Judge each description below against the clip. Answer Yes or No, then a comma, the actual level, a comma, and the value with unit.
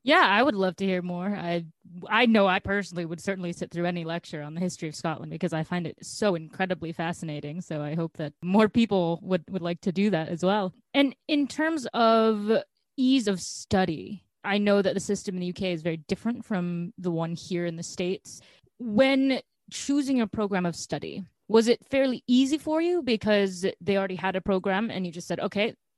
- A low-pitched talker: No, high, 190 Hz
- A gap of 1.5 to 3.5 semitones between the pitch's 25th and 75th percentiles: No, average, 4.1 semitones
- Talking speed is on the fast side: Yes, fast, 210 wpm